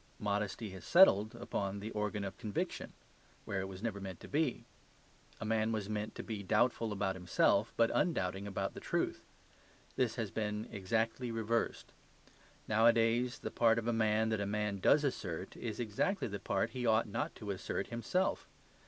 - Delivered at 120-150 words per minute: No, average, 175 wpm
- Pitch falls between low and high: No, low, 110 Hz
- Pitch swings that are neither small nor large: No, narrow, 2.3 semitones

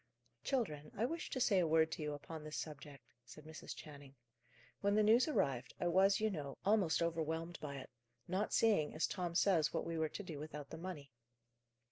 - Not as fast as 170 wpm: No, average, 200 wpm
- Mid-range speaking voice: Yes, medium, 160 Hz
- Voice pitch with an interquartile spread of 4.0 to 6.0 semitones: Yes, average, 4.7 semitones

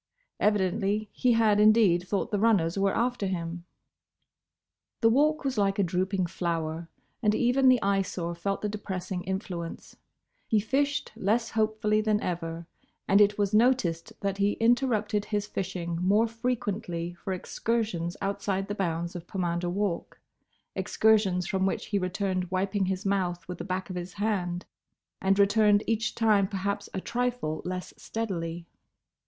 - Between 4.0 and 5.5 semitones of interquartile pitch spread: No, average, 3.1 semitones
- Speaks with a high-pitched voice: Yes, high, 195 Hz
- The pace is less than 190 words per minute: Yes, average, 150 wpm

